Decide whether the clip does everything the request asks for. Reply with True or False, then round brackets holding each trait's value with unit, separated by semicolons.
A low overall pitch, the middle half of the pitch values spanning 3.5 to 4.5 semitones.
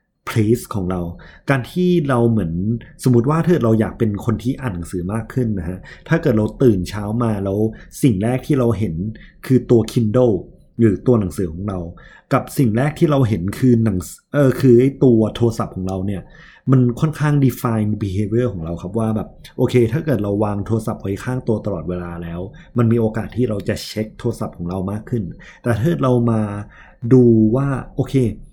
True (115 Hz; 3.8 semitones)